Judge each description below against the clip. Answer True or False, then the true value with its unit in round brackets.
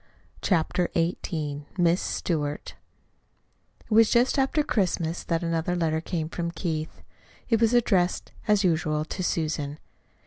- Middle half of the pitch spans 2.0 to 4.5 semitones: True (3.4 semitones)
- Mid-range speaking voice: True (170 Hz)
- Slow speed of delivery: True (130 wpm)